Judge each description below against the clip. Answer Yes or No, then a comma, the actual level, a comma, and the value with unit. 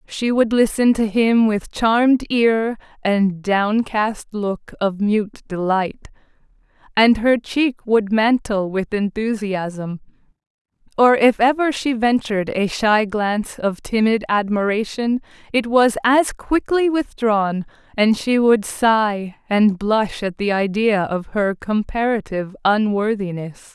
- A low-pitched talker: No, high, 215 Hz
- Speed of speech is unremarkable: No, slow, 125 wpm